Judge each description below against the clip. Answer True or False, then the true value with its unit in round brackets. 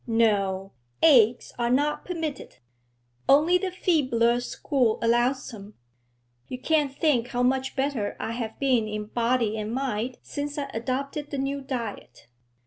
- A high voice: True (255 Hz)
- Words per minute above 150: False (140 wpm)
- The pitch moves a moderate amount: True (3.5 semitones)